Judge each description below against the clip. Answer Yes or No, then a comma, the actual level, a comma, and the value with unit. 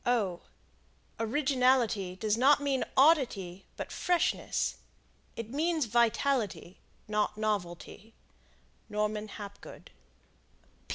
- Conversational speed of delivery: No, slow, 75 wpm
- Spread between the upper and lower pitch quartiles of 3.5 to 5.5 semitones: Yes, average, 4.5 semitones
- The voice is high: Yes, high, 225 Hz